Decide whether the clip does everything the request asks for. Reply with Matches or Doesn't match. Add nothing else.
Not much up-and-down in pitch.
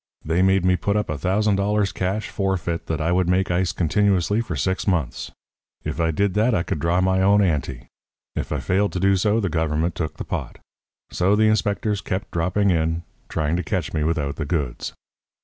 Doesn't match